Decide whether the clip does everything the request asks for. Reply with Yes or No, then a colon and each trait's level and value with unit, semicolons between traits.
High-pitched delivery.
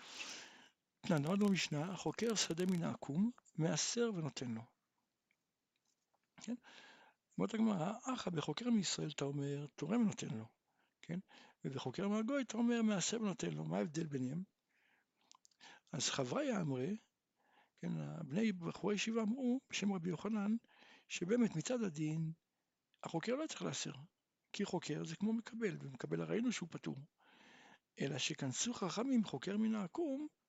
Yes: high, 195 Hz